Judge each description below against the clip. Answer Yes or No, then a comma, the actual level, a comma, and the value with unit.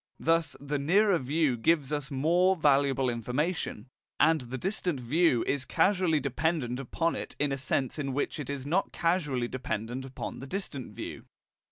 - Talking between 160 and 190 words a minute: Yes, average, 165 wpm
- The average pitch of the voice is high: No, medium, 145 Hz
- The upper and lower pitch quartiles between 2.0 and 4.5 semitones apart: Yes, average, 4.1 semitones